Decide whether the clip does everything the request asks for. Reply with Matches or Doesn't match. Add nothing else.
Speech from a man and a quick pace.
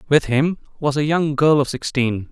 Matches